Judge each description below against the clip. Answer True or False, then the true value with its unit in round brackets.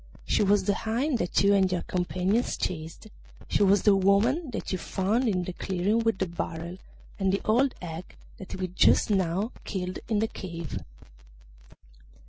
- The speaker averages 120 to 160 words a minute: False (170 wpm)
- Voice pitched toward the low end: False (195 Hz)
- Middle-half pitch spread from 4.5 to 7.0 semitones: False (3.1 semitones)